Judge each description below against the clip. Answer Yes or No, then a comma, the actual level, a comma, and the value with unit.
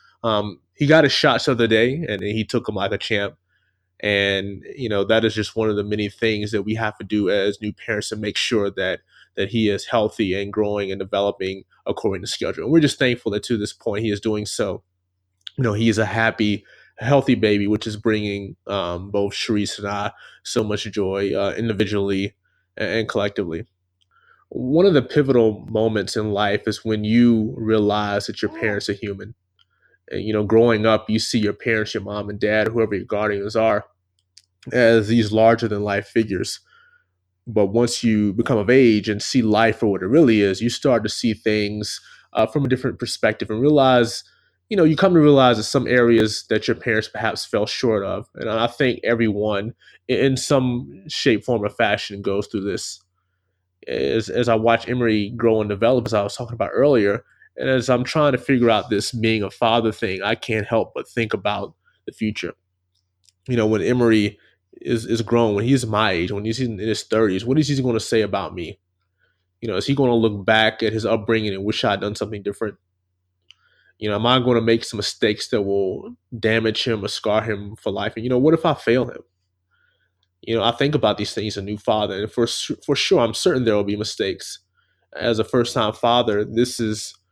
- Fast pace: Yes, fast, 210 wpm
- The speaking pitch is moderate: No, low, 110 Hz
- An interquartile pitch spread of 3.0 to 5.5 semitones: No, narrow, 2.5 semitones